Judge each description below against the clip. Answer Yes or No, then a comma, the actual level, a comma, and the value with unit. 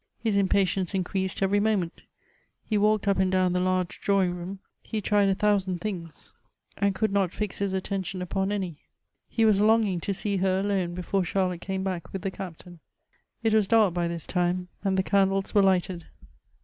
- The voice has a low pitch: No, high, 190 Hz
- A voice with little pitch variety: Yes, narrow, 1.7 semitones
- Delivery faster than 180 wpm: Yes, average, 190 wpm